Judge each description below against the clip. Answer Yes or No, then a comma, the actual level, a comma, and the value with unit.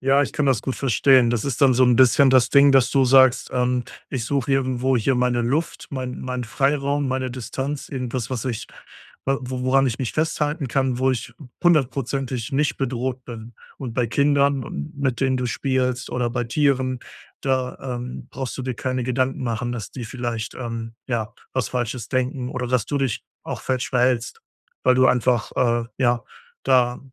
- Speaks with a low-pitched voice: Yes, low, 130 Hz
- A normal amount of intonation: No, narrow, 1.8 semitones